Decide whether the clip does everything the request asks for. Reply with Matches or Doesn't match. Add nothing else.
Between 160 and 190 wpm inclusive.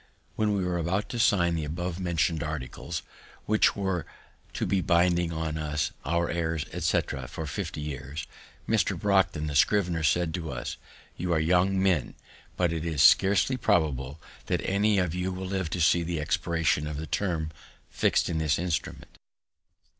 Matches